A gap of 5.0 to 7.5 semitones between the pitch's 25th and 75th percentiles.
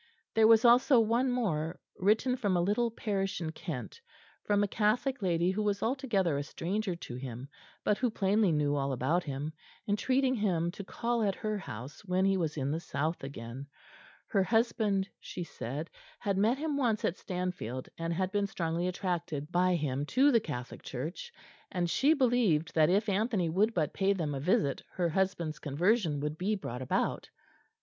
Yes: wide, 5.6 semitones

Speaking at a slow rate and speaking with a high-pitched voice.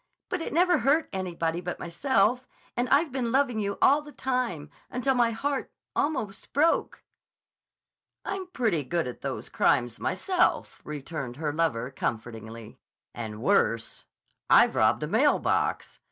Yes: slow, 130 wpm; high, 210 Hz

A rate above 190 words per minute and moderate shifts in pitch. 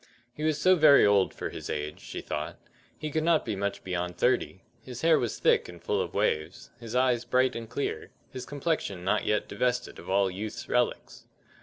No: average, 200 wpm; wide, 6.5 semitones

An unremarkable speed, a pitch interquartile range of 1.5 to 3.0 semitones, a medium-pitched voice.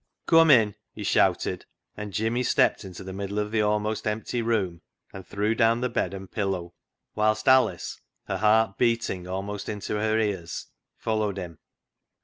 No: average, 160 wpm; narrow, 2.5 semitones; low, 105 Hz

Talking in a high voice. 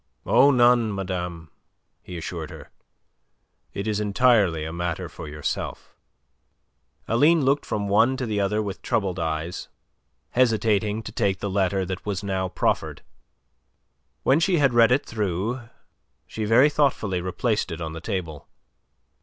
No: low, 100 Hz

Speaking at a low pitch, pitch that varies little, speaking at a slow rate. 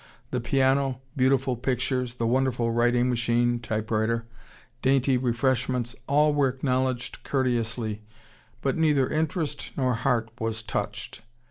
Yes: low, 125 Hz; narrow, 2.1 semitones; slow, 115 wpm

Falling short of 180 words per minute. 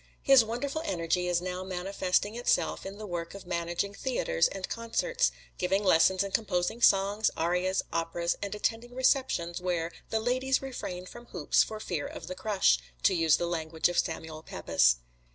Yes: average, 170 wpm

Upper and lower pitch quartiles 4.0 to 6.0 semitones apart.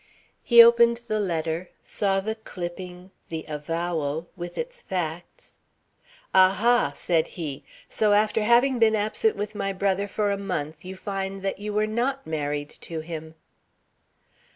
Yes: average, 4.5 semitones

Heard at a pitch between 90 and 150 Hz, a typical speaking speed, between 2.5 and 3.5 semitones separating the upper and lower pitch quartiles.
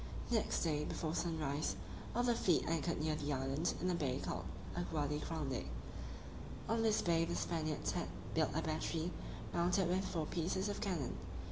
No: medium, 165 Hz; average, 165 wpm; average, 3.0 semitones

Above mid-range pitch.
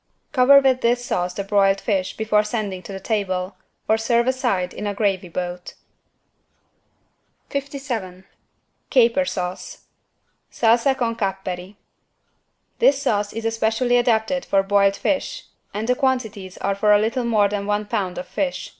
Yes: high, 215 Hz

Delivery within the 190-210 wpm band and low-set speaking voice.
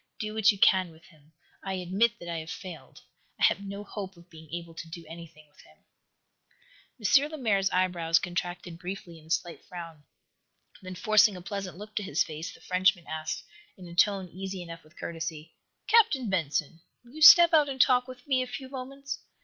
No: average, 200 wpm; medium, 185 Hz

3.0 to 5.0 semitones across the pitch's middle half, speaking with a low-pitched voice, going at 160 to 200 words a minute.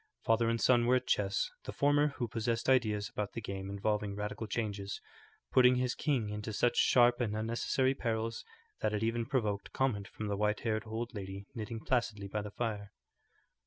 No: narrow, 2.6 semitones; low, 110 Hz; average, 185 wpm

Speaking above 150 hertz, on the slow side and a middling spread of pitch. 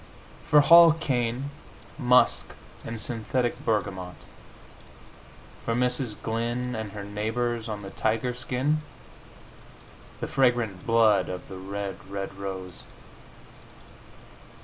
No: low, 115 Hz; slow, 100 wpm; average, 3.7 semitones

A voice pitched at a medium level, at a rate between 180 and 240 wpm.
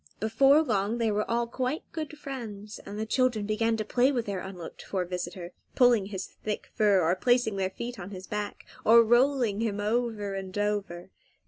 No: high, 215 Hz; average, 190 wpm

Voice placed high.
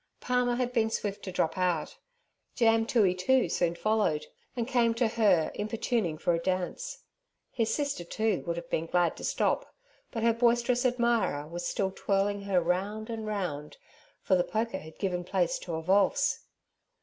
Yes: high, 205 Hz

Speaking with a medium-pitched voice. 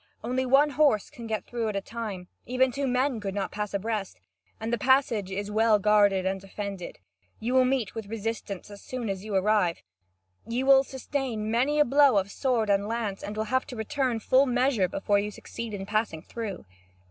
No: high, 220 Hz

